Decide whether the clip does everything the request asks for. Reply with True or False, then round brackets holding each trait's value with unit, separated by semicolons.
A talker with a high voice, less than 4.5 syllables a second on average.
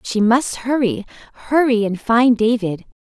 True (230 Hz; 4.3 syllables/s)